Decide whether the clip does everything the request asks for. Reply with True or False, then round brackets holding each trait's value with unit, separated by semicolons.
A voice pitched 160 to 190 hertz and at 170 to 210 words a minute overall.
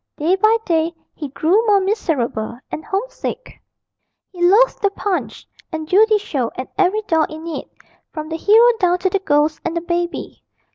False (350 Hz; 175 wpm)